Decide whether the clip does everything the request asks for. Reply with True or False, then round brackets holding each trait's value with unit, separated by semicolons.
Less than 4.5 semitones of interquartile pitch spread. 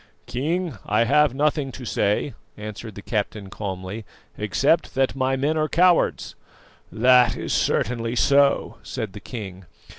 False (5.0 semitones)